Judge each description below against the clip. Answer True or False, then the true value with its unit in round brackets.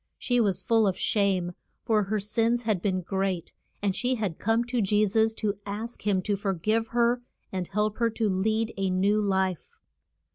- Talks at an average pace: True (190 wpm)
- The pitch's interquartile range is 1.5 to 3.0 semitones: True (2.7 semitones)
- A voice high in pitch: True (210 Hz)